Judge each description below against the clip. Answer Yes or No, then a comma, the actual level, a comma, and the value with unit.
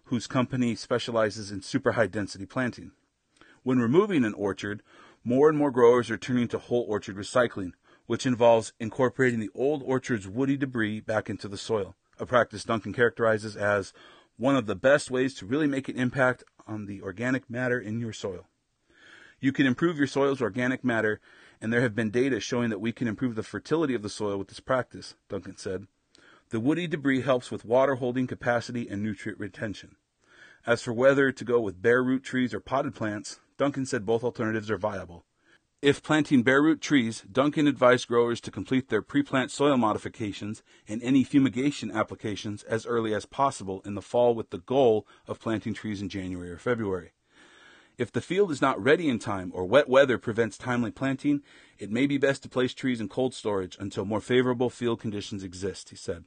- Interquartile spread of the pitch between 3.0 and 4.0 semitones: Yes, average, 3.6 semitones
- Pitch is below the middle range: Yes, low, 120 Hz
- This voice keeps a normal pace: Yes, average, 190 wpm